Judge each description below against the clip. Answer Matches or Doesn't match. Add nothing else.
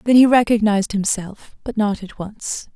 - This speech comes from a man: Doesn't match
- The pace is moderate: Matches